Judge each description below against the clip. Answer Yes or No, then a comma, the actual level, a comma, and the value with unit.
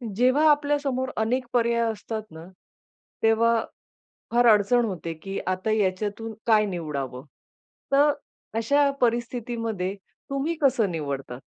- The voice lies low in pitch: No, high, 225 Hz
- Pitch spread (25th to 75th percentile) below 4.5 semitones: No, average, 4.8 semitones